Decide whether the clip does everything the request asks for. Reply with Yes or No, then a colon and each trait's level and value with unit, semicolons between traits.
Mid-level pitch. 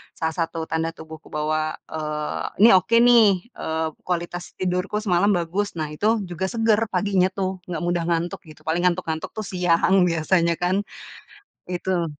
Yes: medium, 175 Hz